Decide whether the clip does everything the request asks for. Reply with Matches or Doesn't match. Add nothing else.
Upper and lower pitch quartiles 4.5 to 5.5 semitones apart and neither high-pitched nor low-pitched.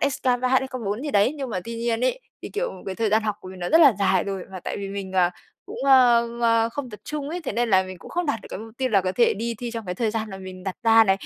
Doesn't match